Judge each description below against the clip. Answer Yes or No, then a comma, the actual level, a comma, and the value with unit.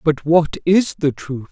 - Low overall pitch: No, medium, 160 Hz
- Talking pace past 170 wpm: Yes, average, 200 wpm